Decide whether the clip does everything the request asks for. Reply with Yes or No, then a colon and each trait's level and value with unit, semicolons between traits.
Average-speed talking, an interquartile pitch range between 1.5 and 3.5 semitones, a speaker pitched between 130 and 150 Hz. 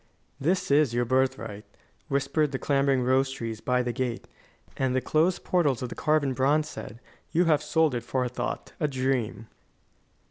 Yes: average, 170 wpm; average, 3.0 semitones; low, 135 Hz